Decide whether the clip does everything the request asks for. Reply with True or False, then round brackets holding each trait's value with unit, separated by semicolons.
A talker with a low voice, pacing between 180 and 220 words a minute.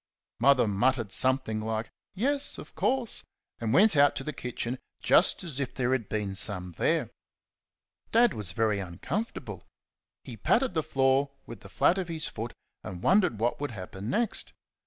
False (130 Hz; 165 wpm)